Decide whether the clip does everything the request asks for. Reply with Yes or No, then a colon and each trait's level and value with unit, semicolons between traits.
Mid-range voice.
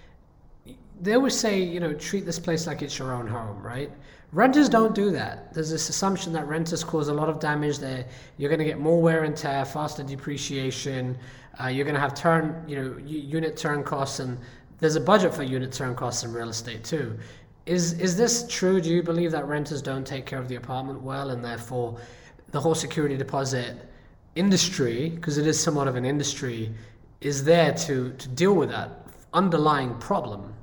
Yes: medium, 145 Hz